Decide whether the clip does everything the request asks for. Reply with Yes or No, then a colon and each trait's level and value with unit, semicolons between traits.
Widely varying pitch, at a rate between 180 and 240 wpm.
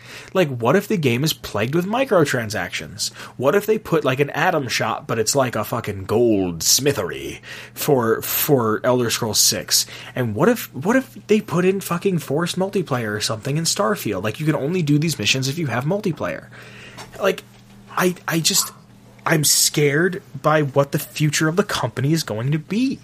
Yes: wide, 6.6 semitones; average, 190 wpm